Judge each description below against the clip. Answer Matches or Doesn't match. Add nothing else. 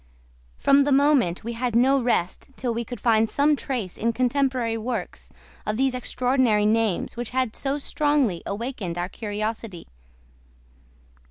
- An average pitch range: Matches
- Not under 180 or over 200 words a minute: Doesn't match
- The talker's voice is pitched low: Doesn't match